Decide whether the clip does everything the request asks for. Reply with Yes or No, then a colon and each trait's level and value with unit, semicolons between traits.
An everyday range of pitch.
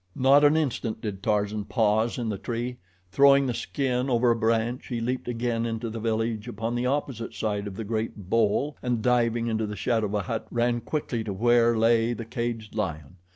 No: narrow, 1.9 semitones